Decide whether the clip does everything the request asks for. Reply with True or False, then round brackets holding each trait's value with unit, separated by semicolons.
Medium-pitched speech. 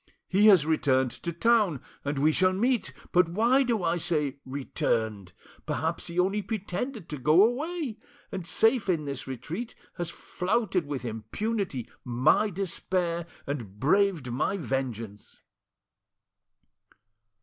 True (170 Hz)